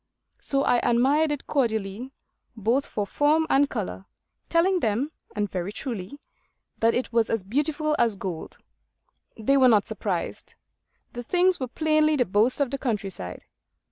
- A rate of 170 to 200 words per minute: No, average, 150 wpm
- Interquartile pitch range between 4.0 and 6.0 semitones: Yes, wide, 5.6 semitones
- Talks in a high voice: Yes, high, 245 Hz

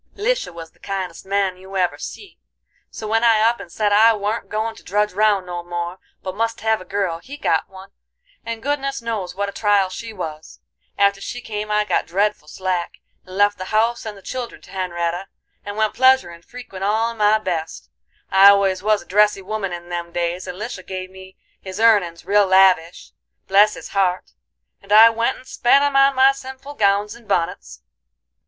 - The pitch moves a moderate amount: Yes, average, 3.2 semitones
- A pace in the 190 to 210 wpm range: Yes, average, 200 wpm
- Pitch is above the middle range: Yes, high, 200 Hz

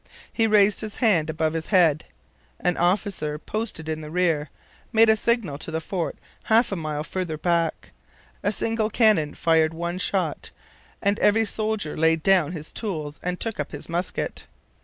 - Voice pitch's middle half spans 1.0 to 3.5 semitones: No, average, 5.0 semitones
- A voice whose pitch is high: No, medium, 175 Hz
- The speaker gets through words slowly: No, average, 170 wpm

